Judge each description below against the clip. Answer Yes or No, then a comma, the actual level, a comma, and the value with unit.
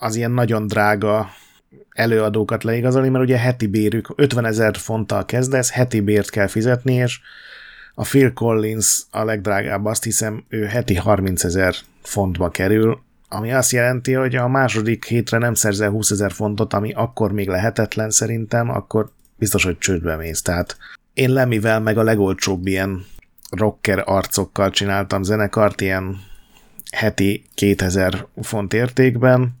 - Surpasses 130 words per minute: Yes, average, 145 wpm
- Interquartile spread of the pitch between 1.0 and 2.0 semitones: No, average, 2.7 semitones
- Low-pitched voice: Yes, low, 110 Hz